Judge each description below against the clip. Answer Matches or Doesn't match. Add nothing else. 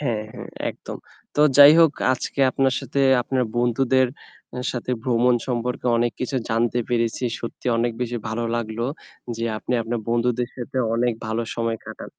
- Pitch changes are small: Matches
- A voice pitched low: Matches